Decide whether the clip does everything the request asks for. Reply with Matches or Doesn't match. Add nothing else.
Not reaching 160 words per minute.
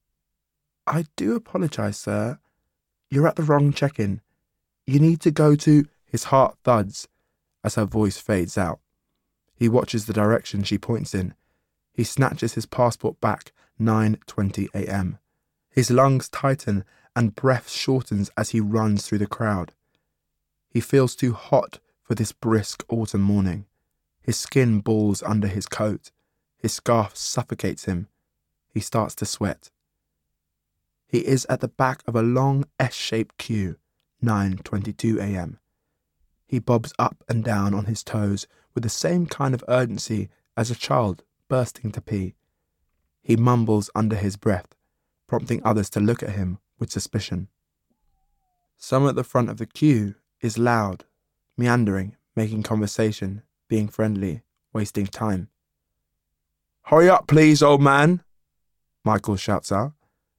Matches